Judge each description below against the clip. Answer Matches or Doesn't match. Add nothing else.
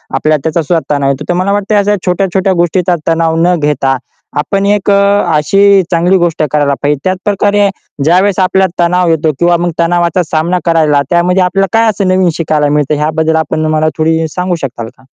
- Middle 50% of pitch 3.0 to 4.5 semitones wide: Matches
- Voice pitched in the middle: Matches